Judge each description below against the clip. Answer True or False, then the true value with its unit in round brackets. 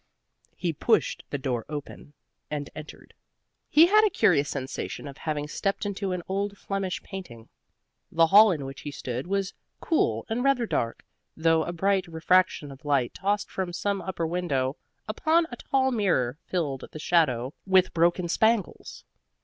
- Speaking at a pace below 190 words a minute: True (160 wpm)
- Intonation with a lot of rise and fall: True (5.7 semitones)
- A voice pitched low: False (175 Hz)